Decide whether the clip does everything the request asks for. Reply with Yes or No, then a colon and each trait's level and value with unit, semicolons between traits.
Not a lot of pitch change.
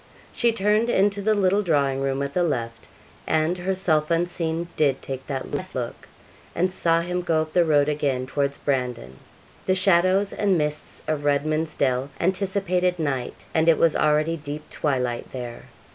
No: average, 4.5 semitones